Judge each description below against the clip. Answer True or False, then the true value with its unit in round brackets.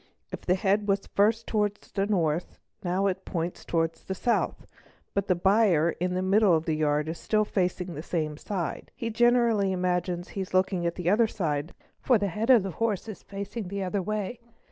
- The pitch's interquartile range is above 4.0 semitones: False (3.2 semitones)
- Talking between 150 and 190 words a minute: False (205 wpm)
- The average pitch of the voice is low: False (190 Hz)